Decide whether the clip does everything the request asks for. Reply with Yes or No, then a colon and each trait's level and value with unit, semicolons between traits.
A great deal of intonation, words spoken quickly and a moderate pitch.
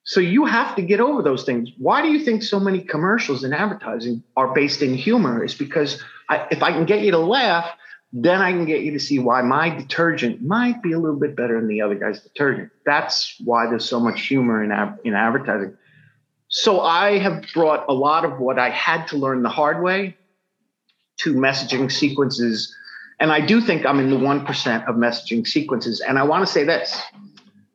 Yes: wide, 6.7 semitones; fast, 210 wpm; medium, 150 Hz